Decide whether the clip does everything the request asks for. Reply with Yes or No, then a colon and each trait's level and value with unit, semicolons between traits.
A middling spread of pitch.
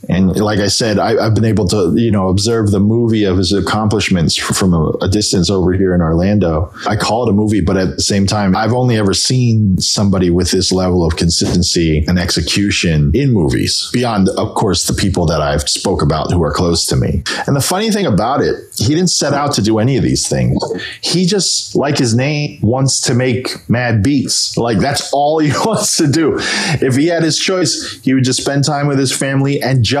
No: wide, 6.4 semitones